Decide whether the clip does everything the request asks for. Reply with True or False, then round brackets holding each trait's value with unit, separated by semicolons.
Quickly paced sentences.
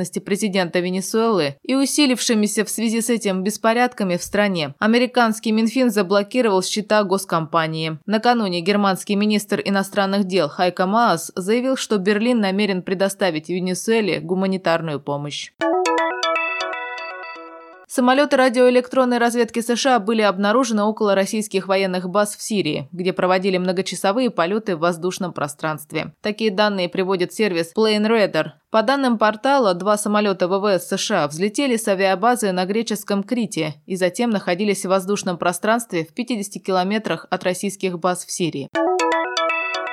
False (125 wpm)